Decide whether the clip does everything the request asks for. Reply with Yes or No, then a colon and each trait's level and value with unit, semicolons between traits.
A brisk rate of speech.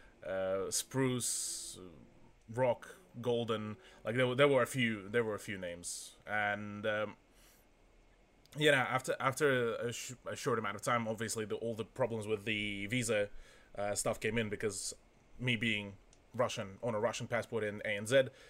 No: average, 160 wpm